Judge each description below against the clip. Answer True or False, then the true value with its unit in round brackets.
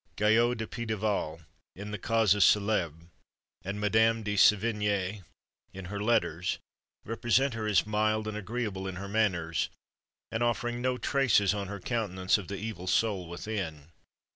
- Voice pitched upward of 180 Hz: False (105 Hz)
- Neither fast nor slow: True (145 wpm)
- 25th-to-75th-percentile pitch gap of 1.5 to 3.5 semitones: True (2.8 semitones)